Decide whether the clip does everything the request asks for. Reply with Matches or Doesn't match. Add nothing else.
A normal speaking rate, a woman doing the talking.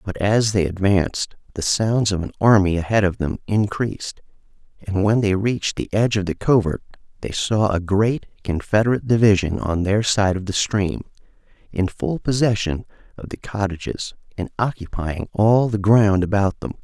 Doesn't match